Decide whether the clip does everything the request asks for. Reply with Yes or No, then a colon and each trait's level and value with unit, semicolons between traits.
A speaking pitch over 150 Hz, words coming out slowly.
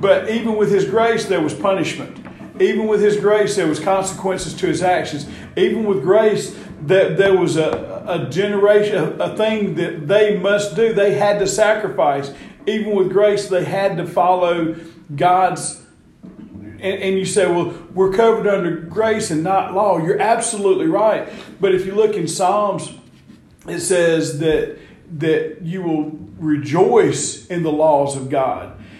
No: high, 190 Hz; average, 155 wpm